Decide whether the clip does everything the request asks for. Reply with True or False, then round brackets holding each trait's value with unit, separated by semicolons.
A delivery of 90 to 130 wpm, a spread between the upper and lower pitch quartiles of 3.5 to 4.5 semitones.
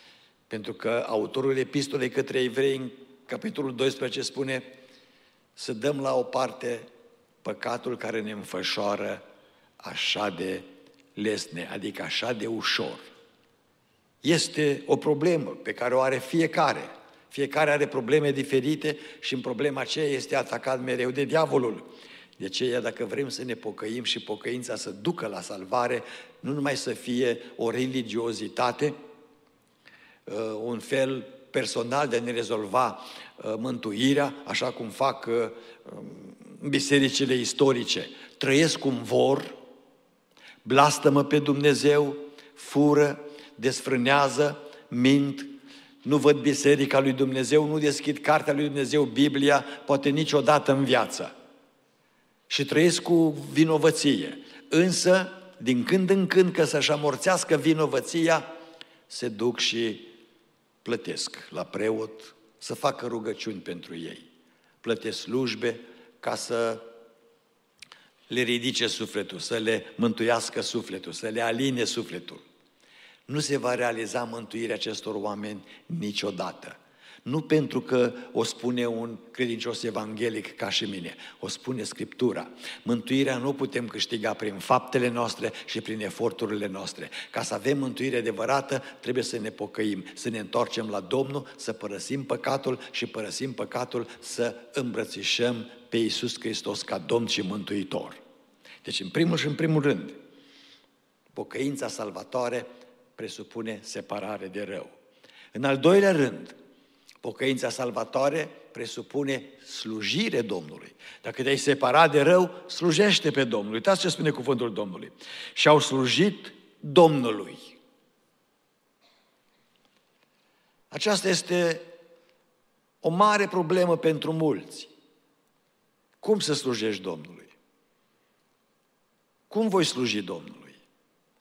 True (120 wpm; 4.0 semitones)